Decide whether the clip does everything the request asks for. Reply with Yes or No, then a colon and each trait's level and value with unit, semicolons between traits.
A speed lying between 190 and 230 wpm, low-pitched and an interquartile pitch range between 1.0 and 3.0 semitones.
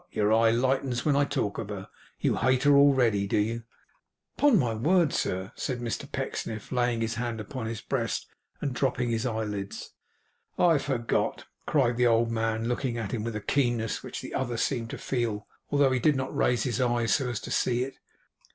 Yes: average, 195 wpm; low, 120 Hz; average, 2.7 semitones